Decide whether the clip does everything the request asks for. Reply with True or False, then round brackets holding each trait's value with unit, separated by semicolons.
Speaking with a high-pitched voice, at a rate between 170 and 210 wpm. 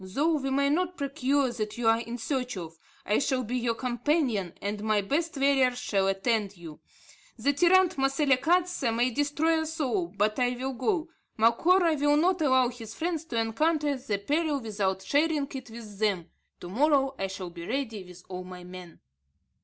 True (255 Hz; 180 wpm)